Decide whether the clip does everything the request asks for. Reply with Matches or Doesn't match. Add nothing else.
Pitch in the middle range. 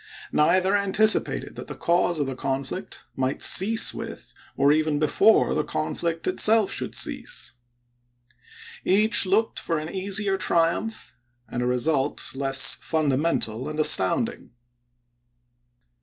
Matches